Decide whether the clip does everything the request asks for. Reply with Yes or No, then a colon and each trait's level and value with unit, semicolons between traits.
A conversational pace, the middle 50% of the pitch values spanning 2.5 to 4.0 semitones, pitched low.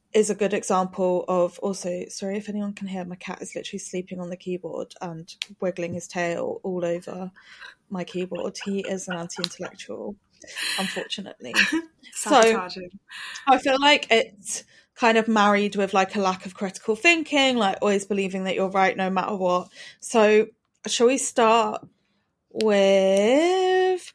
No: average, 155 wpm; average, 3.5 semitones; high, 195 Hz